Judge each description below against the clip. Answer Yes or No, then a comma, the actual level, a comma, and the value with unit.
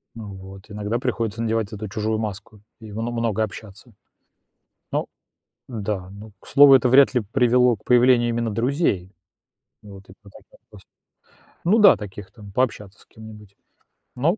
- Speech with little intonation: No, average, 3.0 semitones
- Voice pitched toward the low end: Yes, low, 110 Hz